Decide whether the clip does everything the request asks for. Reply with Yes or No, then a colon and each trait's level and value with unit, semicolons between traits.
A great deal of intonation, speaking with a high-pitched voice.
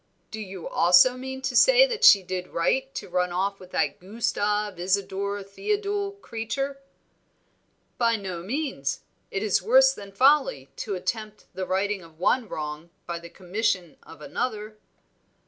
Yes: wide, 5.9 semitones; high, 205 Hz